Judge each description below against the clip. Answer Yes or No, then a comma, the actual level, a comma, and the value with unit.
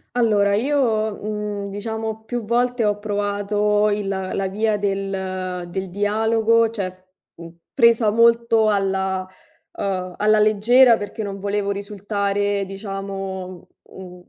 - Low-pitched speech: No, high, 205 Hz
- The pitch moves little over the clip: Yes, narrow, 2.1 semitones